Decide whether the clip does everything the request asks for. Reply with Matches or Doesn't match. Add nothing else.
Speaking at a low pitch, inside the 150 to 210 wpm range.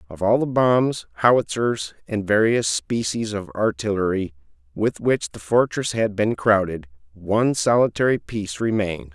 Doesn't match